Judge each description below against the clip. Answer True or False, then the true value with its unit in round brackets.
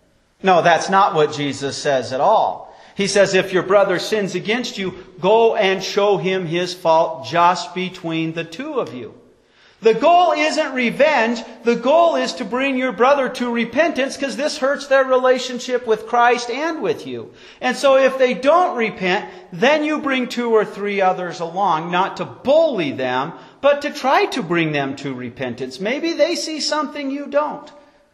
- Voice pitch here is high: True (235 Hz)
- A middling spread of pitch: False (7.7 semitones)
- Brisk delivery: False (175 wpm)